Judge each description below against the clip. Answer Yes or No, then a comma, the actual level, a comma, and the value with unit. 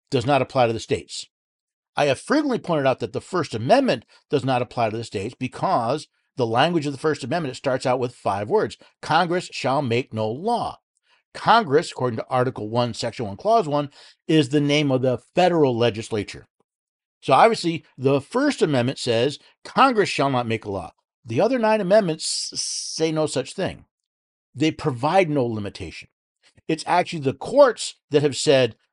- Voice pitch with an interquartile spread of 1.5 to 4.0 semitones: No, average, 4.7 semitones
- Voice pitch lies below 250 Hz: Yes, low, 135 Hz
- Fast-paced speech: No, average, 185 wpm